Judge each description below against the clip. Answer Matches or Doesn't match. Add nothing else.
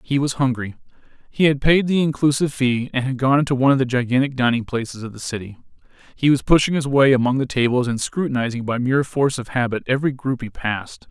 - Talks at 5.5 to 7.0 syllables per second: Matches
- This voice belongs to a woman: Doesn't match